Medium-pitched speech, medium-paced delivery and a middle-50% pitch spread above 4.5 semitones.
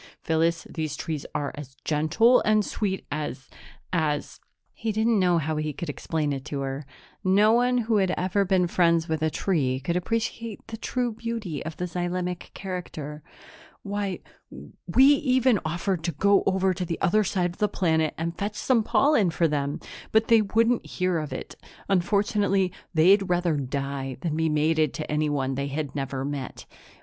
Yes: medium, 175 Hz; average, 175 wpm; average, 5.0 semitones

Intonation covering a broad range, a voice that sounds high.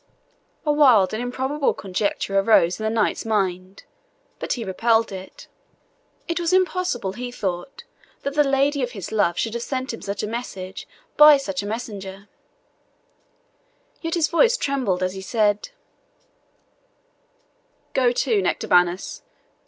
Yes: wide, 5.9 semitones; high, 225 Hz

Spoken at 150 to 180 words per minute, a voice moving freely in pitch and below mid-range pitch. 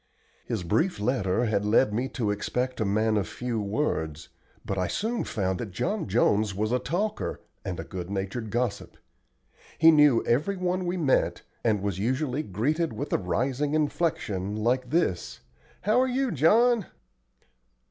Yes: average, 160 wpm; wide, 7.3 semitones; low, 120 Hz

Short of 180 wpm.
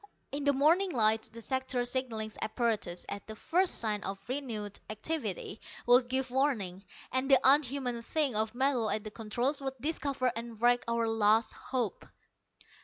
Yes: average, 160 wpm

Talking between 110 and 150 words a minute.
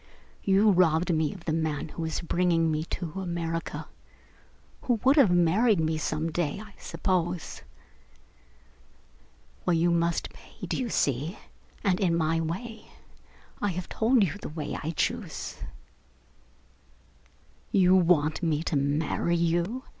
Yes: average, 140 wpm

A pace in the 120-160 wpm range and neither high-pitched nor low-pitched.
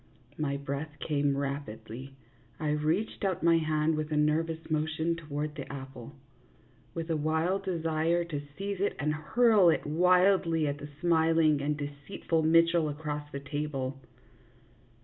Yes: average, 145 wpm; medium, 155 Hz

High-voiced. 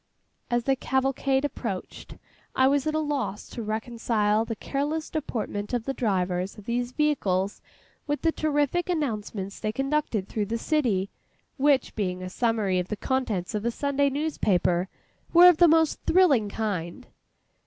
Yes: high, 240 Hz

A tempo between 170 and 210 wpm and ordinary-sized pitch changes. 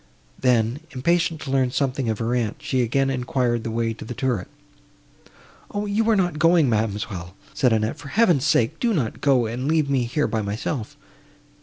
Yes: average, 185 wpm; average, 4.8 semitones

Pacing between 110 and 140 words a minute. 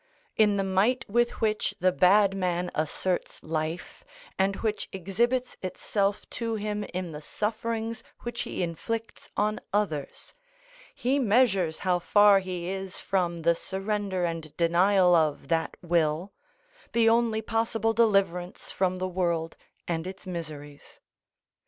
Yes: slow, 135 wpm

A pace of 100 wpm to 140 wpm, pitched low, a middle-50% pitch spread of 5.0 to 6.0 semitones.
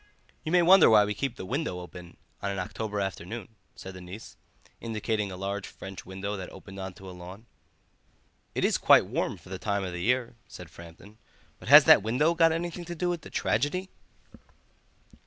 No: average, 200 wpm; low, 105 Hz; wide, 5.5 semitones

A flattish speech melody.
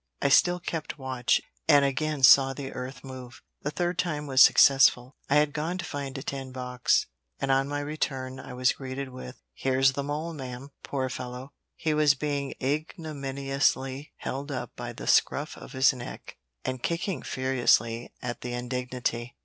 Yes: narrow, 2.1 semitones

